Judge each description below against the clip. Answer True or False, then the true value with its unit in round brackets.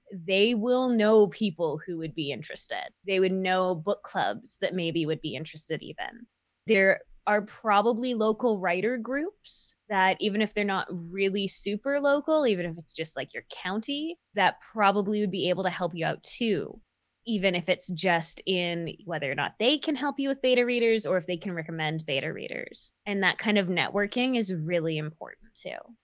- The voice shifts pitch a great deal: False (4.6 semitones)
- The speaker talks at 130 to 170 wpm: False (185 wpm)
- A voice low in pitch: False (195 Hz)